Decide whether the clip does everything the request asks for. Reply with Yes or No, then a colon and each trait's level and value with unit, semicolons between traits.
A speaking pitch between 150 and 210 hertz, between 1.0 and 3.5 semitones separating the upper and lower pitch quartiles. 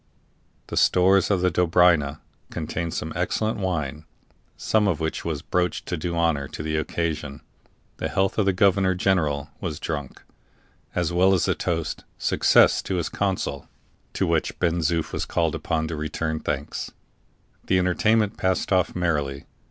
No: very low, 85 Hz; average, 3.2 semitones